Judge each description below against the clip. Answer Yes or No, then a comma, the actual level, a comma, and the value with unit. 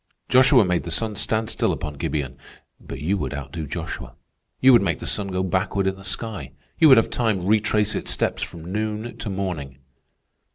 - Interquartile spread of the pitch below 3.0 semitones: No, average, 5.0 semitones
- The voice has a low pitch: Yes, very low, 95 Hz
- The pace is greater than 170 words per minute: Yes, average, 195 wpm